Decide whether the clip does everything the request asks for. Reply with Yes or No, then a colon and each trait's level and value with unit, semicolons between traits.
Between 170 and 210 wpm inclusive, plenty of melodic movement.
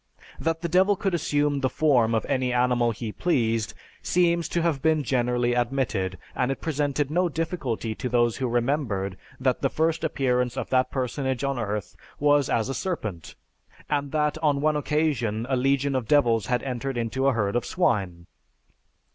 No: average, 175 wpm; average, 4.0 semitones